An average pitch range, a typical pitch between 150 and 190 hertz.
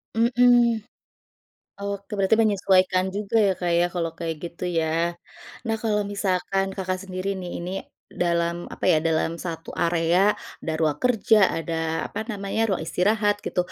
Yes: average, 3.1 semitones; medium, 185 Hz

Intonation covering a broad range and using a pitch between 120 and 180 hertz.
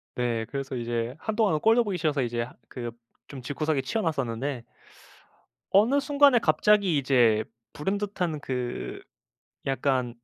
Yes: wide, 8.4 semitones; medium, 140 Hz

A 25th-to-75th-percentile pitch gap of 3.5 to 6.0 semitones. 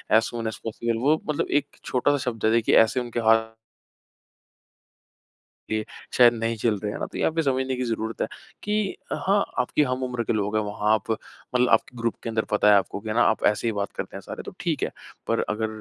No: narrow, 2.5 semitones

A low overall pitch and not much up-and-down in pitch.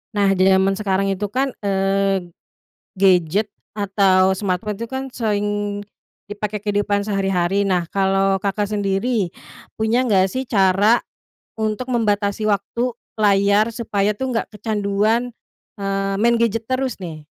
No: high, 205 Hz; narrow, 2.1 semitones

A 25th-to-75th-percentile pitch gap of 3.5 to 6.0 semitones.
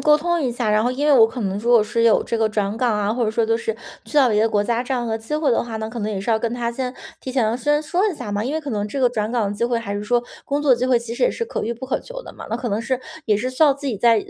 No: average, 3.1 semitones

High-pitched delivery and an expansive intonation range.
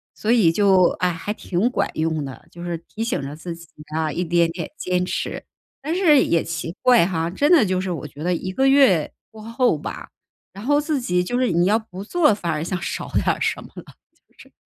No: medium, 180 Hz; wide, 5.8 semitones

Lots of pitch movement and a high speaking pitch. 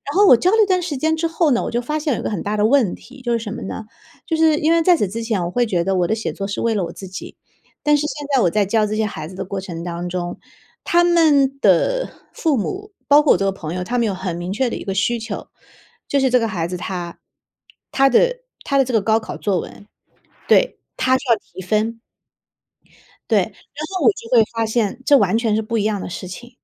Yes: wide, 6.5 semitones; high, 230 Hz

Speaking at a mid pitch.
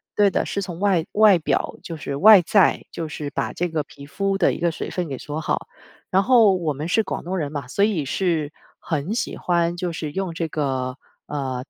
Yes: medium, 170 Hz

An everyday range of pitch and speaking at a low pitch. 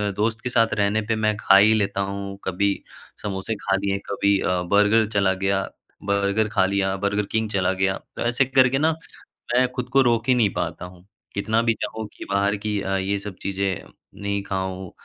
No: narrow, 2.2 semitones; low, 100 Hz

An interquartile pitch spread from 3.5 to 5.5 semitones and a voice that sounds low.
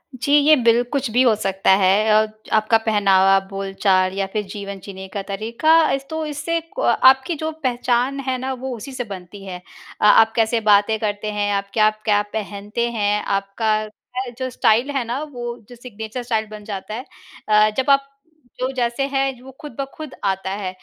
No: average, 4.0 semitones; high, 220 Hz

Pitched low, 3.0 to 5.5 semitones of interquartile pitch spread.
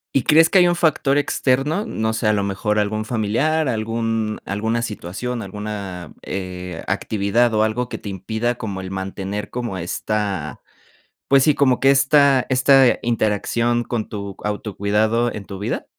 Yes: low, 110 Hz; average, 3.7 semitones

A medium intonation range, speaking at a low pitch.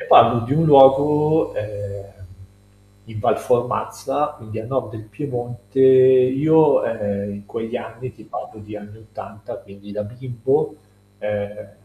Yes: average, 4.2 semitones; low, 115 Hz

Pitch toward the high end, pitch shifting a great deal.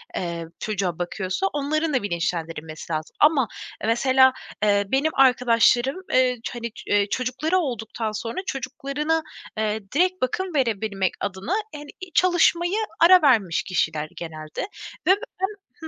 Yes: high, 245 Hz; wide, 7.2 semitones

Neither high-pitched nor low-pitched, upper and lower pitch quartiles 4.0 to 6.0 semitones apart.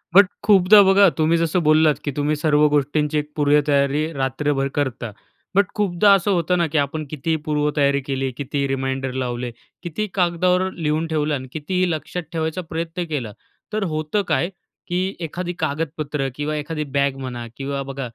No: medium, 150 Hz; average, 3.5 semitones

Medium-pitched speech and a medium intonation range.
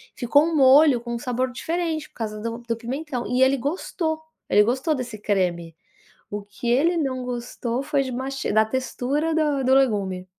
No: very high, 255 Hz; average, 3.9 semitones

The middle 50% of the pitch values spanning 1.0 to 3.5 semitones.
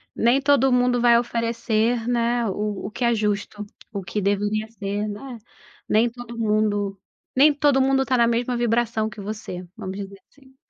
Yes: average, 2.8 semitones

